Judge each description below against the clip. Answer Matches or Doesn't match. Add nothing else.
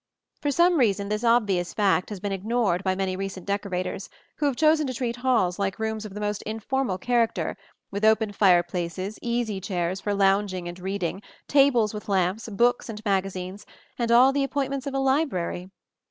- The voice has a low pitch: Doesn't match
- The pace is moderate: Matches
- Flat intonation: Doesn't match